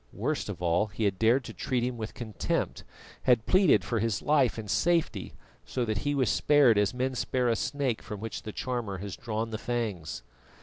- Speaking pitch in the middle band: No, low, 115 Hz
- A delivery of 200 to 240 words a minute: Yes, fast, 205 wpm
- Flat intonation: No, average, 3.4 semitones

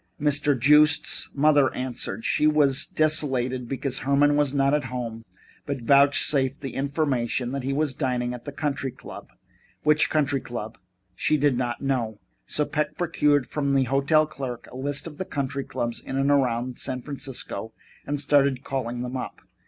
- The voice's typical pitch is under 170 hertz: Yes, low, 135 Hz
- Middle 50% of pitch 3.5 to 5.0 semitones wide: No, narrow, 2.5 semitones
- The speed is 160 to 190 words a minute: Yes, average, 170 wpm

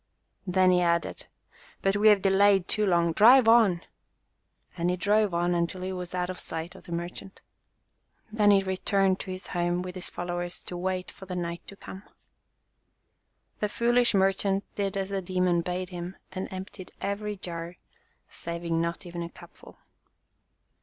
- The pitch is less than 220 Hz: Yes, medium, 185 Hz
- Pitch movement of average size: No, narrow, 2.0 semitones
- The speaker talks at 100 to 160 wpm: No, average, 175 wpm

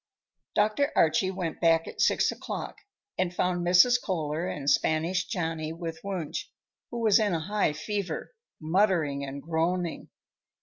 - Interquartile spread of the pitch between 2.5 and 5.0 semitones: Yes, average, 3.5 semitones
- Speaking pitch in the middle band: Yes, medium, 175 Hz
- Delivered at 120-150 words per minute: Yes, average, 140 wpm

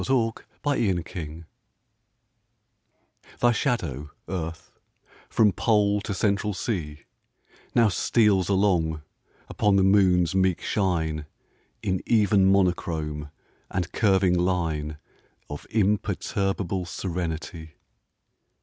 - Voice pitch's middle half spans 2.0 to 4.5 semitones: Yes, average, 3.8 semitones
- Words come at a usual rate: No, slow, 95 wpm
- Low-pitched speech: Yes, very low, 95 Hz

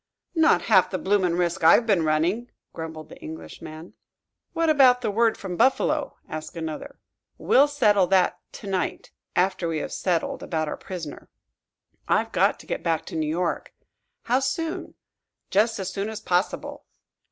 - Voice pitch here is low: No, medium, 185 Hz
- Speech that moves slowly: No, average, 160 wpm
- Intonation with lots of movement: Yes, wide, 5.7 semitones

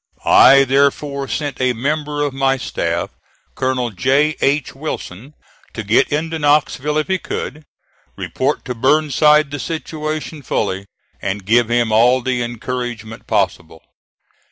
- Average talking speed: No, slow, 130 wpm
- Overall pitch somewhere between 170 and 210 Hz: No, low, 135 Hz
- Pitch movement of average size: Yes, average, 3.9 semitones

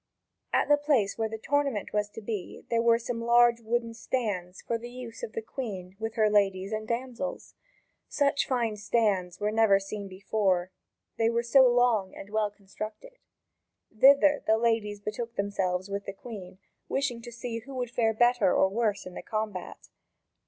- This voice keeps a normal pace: Yes, average, 175 wpm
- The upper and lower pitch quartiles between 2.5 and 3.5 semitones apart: Yes, average, 3.0 semitones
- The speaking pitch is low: No, high, 225 Hz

